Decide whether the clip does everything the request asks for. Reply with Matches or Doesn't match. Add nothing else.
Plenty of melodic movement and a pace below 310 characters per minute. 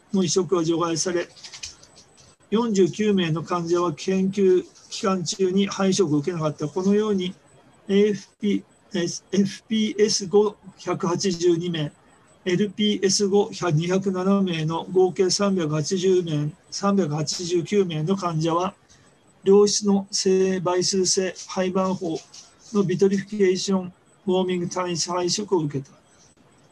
Doesn't match